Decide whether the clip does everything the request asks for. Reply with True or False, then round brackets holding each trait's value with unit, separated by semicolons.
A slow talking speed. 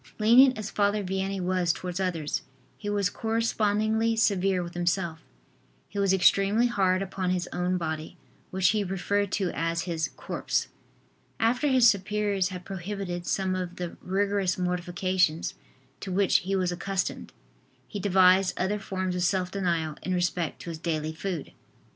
False (155 wpm)